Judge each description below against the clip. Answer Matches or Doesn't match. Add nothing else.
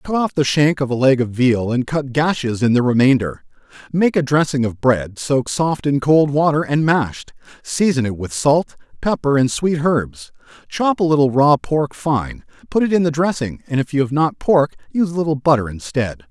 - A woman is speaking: Doesn't match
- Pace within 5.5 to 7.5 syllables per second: Doesn't match